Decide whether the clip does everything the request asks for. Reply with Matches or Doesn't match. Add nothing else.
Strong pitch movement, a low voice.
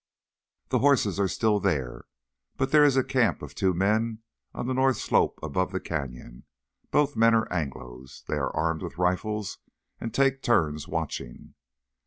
Matches